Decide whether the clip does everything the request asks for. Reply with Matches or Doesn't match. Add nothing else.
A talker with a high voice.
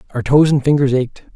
Doesn't match